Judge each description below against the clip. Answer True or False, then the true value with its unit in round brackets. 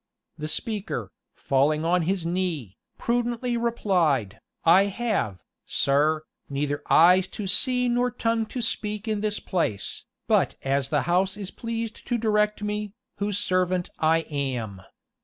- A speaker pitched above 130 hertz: True (185 Hz)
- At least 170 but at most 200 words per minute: False (140 wpm)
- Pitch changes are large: True (6.3 semitones)